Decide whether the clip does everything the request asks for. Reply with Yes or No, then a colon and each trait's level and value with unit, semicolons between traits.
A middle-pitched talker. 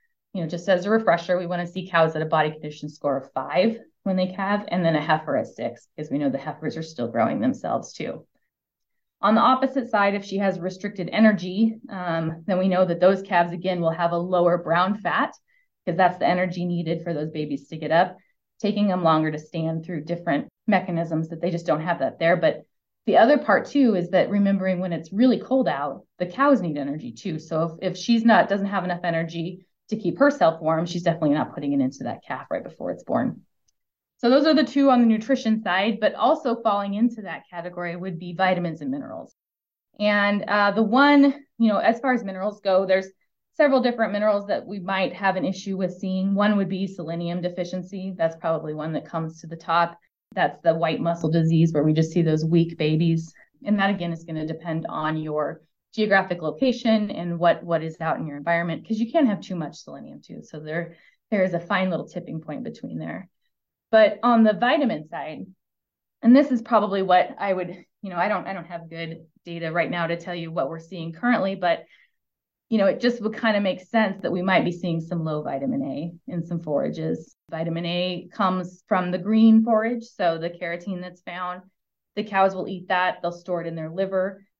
Yes: medium, 180 Hz